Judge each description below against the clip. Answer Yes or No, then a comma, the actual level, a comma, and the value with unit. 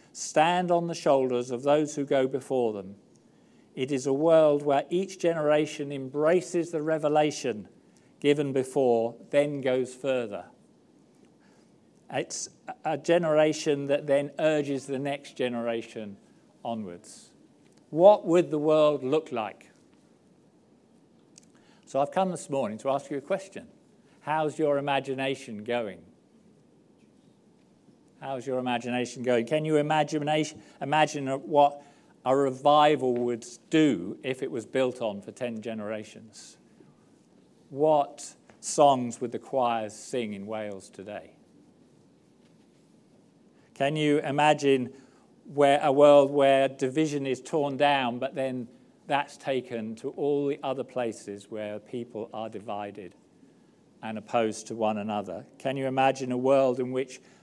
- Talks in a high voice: No, low, 135 Hz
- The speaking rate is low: Yes, slow, 125 wpm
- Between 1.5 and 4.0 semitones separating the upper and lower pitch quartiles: Yes, average, 3.5 semitones